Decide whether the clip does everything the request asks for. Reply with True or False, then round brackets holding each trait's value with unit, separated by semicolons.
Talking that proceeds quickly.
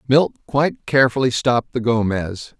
False (140 wpm)